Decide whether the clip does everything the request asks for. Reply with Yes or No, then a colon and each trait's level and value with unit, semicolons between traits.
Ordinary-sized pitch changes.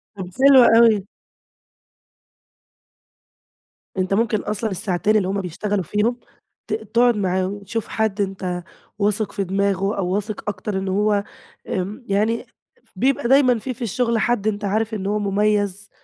No: narrow, 2.3 semitones